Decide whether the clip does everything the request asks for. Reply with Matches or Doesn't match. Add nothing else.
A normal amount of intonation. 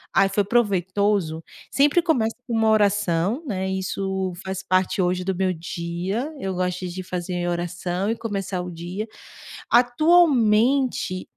Matches